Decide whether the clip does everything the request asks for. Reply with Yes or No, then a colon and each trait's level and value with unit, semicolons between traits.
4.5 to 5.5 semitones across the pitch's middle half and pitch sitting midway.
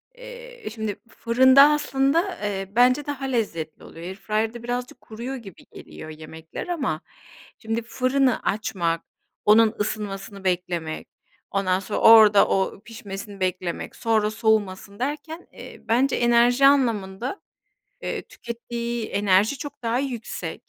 No: average, 4.8 semitones; high, 225 Hz